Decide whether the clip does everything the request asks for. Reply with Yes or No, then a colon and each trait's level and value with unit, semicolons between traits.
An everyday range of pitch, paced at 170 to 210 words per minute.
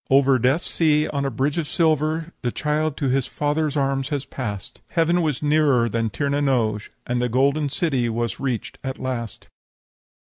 Yes: average, 3.5 semitones; average, 180 wpm